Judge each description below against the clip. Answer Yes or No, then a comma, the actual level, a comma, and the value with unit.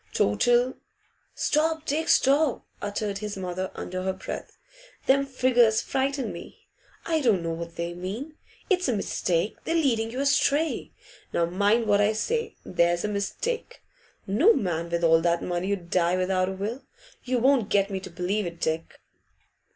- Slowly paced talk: No, average, 165 wpm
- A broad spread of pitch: Yes, wide, 6.9 semitones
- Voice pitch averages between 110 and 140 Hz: No, high, 205 Hz